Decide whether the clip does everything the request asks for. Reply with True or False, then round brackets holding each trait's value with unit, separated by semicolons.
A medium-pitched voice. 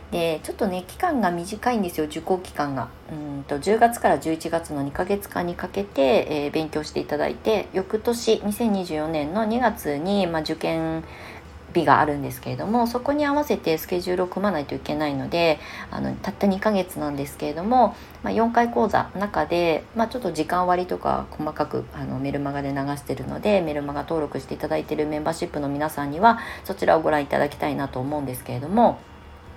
True (160 Hz)